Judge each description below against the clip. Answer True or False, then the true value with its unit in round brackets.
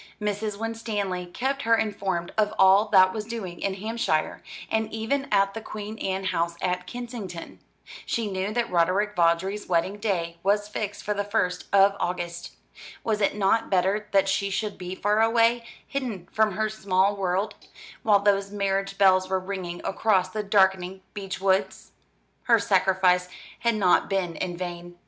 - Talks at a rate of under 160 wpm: False (165 wpm)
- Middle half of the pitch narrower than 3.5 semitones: True (2.5 semitones)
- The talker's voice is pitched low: False (195 Hz)